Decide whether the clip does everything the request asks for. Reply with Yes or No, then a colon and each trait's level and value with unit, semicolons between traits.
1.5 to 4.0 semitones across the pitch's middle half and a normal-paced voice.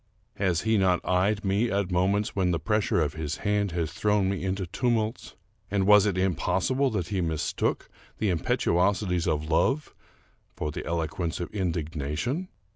Yes: average, 3.5 semitones; average, 160 wpm